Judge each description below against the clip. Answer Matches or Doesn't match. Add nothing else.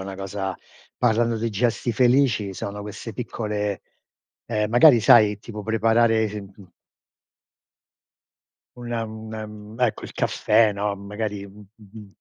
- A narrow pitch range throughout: Matches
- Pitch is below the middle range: Matches